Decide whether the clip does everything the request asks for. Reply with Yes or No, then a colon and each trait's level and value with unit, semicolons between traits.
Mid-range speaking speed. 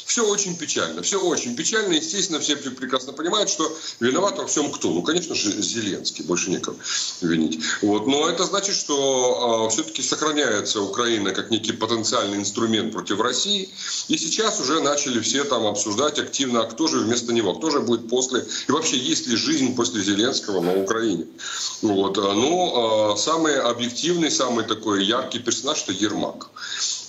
No: fast, 165 wpm